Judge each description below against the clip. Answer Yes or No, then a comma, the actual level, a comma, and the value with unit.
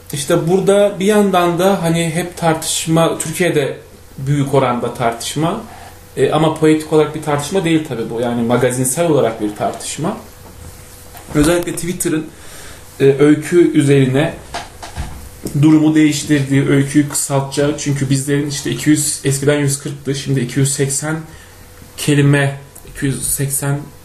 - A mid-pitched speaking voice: Yes, medium, 145 Hz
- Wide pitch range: No, average, 3.4 semitones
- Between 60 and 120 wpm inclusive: Yes, average, 110 wpm